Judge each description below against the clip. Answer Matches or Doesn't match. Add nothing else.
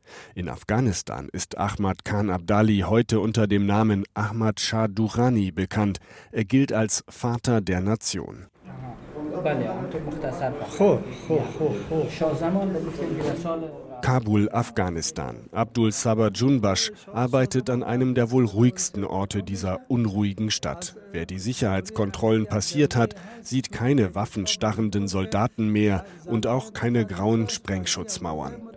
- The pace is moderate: Doesn't match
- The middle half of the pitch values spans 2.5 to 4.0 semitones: Matches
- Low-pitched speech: Matches